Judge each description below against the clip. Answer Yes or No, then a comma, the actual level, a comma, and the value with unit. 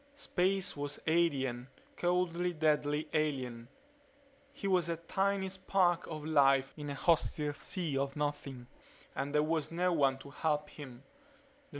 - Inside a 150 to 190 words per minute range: No, slow, 135 wpm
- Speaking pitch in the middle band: Yes, medium, 155 Hz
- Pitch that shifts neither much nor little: Yes, average, 3.8 semitones